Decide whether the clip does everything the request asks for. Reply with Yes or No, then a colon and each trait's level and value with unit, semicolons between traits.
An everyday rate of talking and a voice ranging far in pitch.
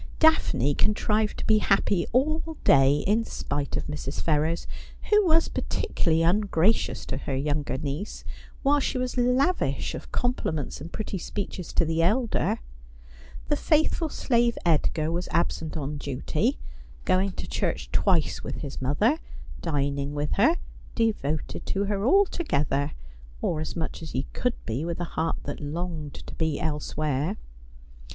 Yes: average, 150 wpm; wide, 7.4 semitones